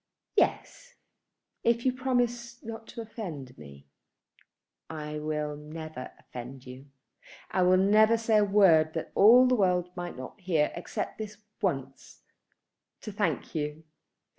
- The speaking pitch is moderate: Yes, medium, 180 Hz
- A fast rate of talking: No, slow, 135 wpm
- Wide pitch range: Yes, wide, 6.8 semitones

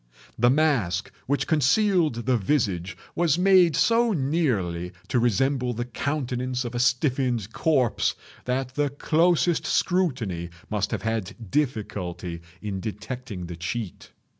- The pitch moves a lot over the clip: Yes, wide, 6.1 semitones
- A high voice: No, low, 125 Hz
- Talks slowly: Yes, slow, 125 wpm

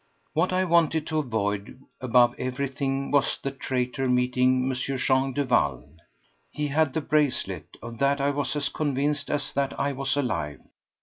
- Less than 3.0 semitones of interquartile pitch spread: Yes, narrow, 2.4 semitones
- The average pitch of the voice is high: No, low, 135 Hz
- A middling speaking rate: Yes, average, 150 wpm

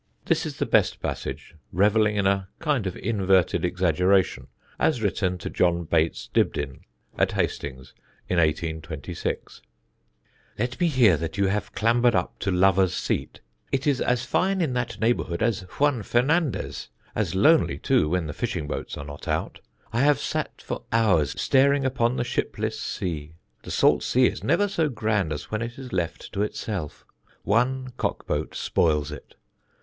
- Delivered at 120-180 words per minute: Yes, average, 165 wpm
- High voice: No, low, 100 Hz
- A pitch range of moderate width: No, wide, 6.3 semitones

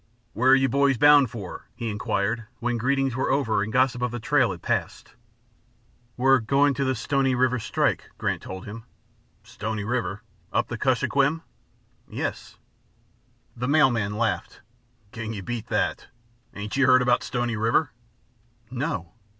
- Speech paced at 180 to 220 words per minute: No, average, 155 wpm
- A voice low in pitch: Yes, low, 120 Hz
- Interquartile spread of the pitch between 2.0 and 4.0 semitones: Yes, average, 3.3 semitones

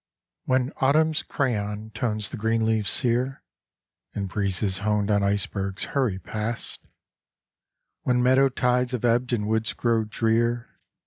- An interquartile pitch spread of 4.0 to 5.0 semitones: No, average, 3.1 semitones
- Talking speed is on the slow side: Yes, slow, 130 wpm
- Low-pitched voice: Yes, low, 115 Hz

